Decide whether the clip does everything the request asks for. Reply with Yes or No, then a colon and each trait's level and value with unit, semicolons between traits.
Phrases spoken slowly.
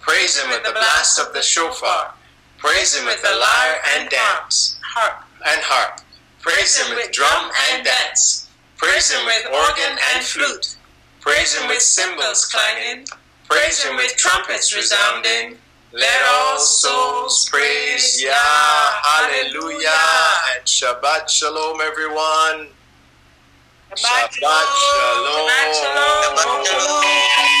Yes: slow, 125 wpm